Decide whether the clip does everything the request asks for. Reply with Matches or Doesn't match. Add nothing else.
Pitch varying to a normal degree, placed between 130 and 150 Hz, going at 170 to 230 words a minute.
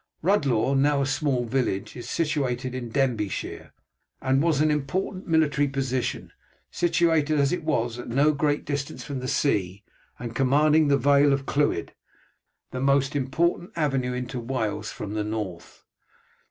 Doesn't match